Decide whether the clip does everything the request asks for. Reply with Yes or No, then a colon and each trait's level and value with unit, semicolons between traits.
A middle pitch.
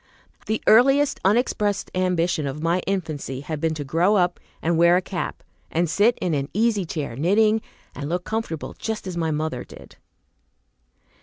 Yes: medium, 175 Hz